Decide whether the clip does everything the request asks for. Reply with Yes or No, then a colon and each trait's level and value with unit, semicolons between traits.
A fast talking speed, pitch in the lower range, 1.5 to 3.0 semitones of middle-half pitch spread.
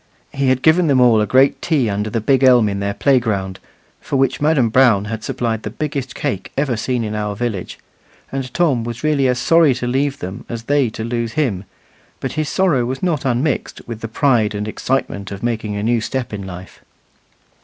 No: fast, 210 wpm; low, 120 Hz; average, 4.1 semitones